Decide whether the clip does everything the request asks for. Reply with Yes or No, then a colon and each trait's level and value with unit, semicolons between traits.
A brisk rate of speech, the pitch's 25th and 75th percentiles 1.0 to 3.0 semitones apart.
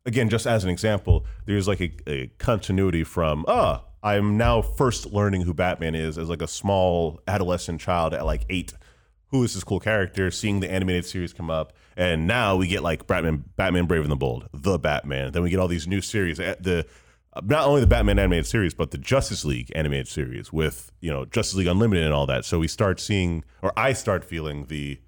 No: fast, 220 wpm; average, 3.9 semitones